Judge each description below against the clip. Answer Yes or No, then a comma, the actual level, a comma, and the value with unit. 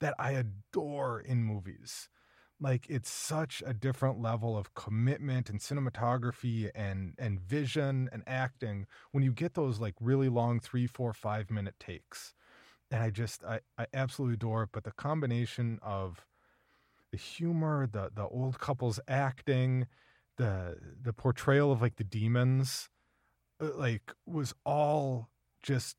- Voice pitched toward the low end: Yes, low, 125 Hz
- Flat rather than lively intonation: No, average, 3.2 semitones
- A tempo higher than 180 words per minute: No, average, 145 wpm